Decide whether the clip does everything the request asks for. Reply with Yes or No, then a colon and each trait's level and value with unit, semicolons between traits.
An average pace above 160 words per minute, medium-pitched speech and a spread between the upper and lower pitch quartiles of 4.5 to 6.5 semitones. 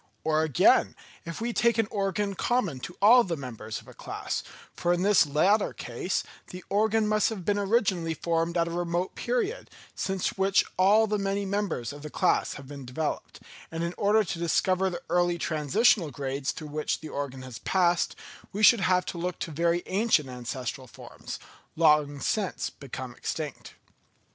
Yes: average, 175 wpm; medium, 175 Hz; average, 5.1 semitones